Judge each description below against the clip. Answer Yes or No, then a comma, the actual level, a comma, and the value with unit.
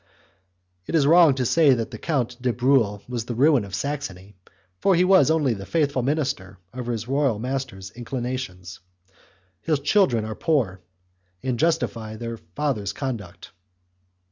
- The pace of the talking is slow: No, average, 150 wpm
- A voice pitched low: Yes, low, 125 Hz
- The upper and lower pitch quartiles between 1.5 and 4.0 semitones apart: No, average, 4.9 semitones